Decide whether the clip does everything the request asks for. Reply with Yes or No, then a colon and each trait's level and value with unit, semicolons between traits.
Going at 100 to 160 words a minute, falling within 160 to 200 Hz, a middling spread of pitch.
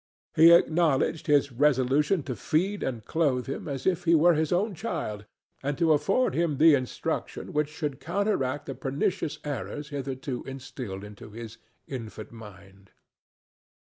No: average, 150 wpm; medium, 145 Hz; average, 4.3 semitones